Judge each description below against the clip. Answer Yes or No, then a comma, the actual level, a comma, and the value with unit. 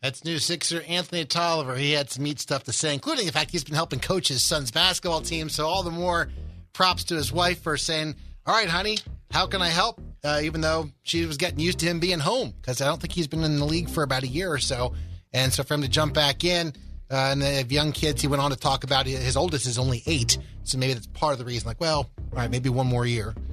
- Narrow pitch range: No, average, 4.2 semitones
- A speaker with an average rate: No, fast, 270 wpm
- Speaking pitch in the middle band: Yes, medium, 150 Hz